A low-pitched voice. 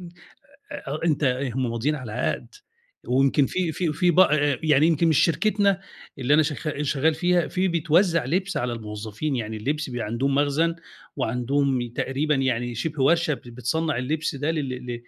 No: medium, 145 Hz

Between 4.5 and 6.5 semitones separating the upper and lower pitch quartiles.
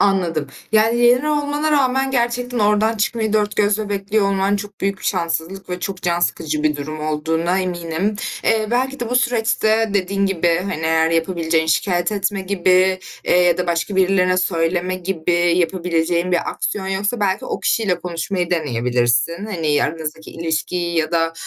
No: average, 4.0 semitones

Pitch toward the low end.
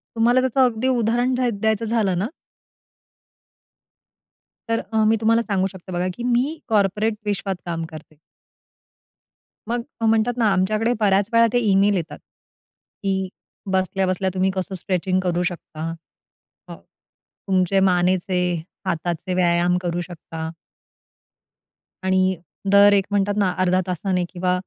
No: high, 190 Hz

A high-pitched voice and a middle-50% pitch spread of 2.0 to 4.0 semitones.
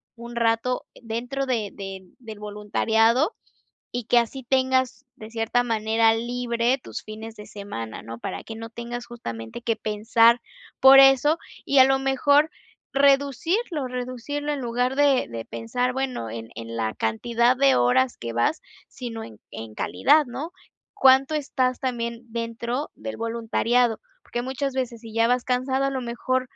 Yes: high, 240 Hz; average, 2.9 semitones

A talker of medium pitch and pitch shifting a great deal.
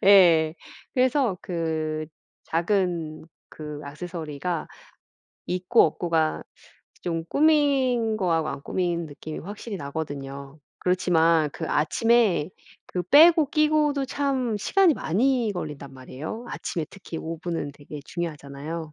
Yes: medium, 170 Hz; wide, 6.6 semitones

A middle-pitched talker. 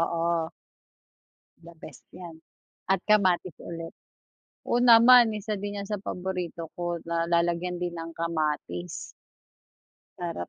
Yes: medium, 175 Hz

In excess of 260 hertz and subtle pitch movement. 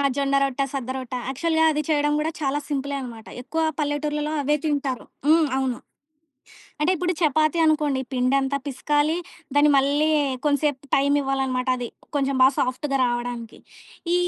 Yes: very high, 280 Hz; narrow, 2.3 semitones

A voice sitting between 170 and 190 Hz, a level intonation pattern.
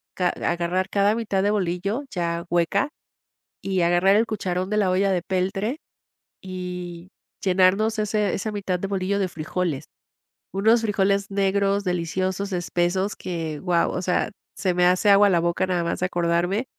Yes: medium, 185 Hz; narrow, 2.2 semitones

